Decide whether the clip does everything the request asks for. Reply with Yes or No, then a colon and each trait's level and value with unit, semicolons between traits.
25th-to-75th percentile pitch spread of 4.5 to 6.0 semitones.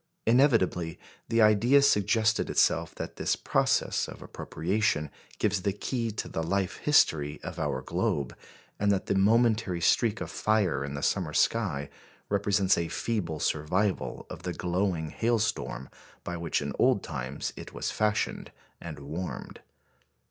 Yes: average, 5.0 semitones